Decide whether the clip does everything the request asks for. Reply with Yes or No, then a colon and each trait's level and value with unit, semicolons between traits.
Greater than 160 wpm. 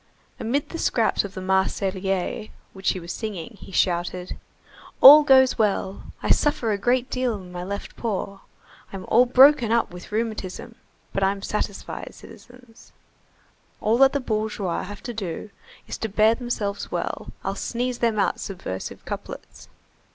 No: average, 155 wpm